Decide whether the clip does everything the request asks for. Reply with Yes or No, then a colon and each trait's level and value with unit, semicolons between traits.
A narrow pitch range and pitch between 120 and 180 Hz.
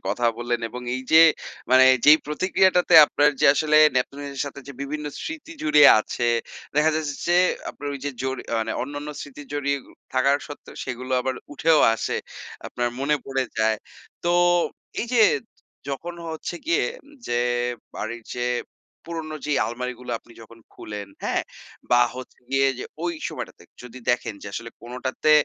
No: average, 3.5 semitones; low, 135 Hz